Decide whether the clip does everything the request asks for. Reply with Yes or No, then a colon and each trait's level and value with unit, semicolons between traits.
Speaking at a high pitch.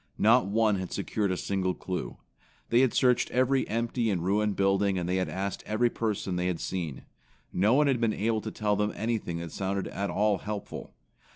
No: low, 105 Hz